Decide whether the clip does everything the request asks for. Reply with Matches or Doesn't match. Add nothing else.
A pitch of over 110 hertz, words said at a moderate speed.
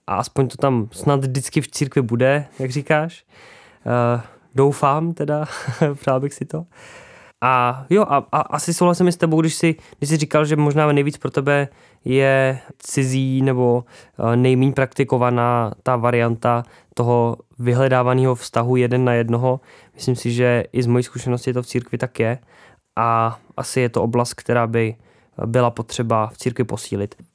Matches